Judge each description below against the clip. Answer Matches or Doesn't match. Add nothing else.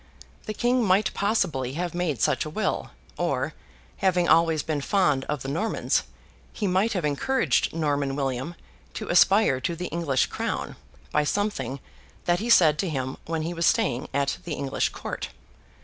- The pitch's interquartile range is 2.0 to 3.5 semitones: Doesn't match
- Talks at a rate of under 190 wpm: Matches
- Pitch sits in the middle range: Matches